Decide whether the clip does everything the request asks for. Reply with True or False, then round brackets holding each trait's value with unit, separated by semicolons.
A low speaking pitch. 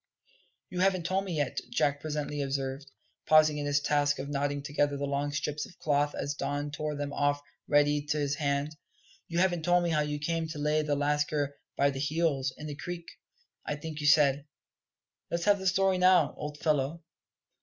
False (150 Hz)